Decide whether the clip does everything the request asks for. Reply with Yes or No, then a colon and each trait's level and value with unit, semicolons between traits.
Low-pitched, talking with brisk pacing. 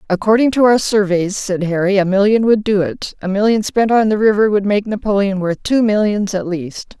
No: high, 200 Hz; fast, 215 wpm